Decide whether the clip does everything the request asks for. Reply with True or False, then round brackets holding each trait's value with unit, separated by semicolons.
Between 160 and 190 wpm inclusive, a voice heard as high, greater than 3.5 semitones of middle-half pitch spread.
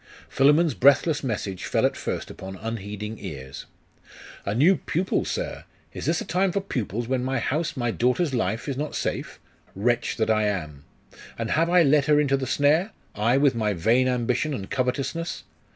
False (180 wpm; 130 Hz; 5.3 semitones)